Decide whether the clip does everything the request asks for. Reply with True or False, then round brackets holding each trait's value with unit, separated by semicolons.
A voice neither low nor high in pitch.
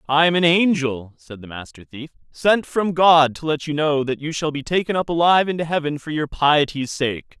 True (150 Hz)